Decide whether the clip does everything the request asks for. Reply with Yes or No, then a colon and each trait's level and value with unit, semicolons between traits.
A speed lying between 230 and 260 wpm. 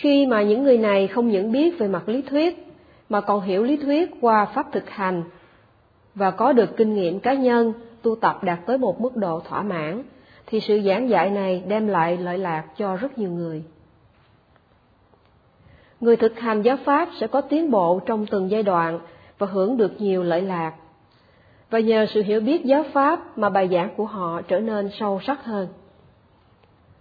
No: average, 190 wpm